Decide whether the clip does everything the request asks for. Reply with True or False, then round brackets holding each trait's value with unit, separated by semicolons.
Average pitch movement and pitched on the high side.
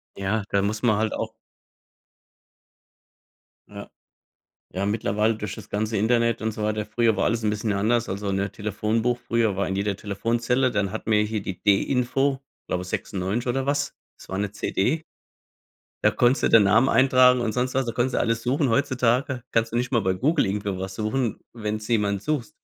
False (3.0 semitones; 110 Hz)